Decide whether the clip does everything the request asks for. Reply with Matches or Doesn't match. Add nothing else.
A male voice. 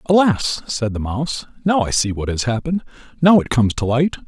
Matches